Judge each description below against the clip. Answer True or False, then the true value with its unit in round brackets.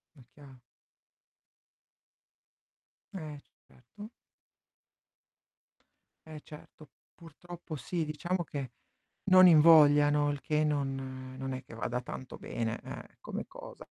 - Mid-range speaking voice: True (150 Hz)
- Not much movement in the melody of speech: False (3.6 semitones)